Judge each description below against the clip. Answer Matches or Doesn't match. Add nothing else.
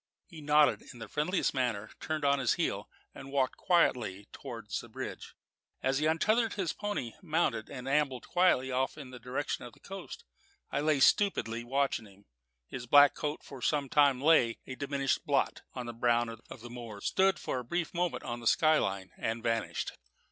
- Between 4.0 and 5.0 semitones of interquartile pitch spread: Matches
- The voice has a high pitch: Doesn't match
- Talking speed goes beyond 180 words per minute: Matches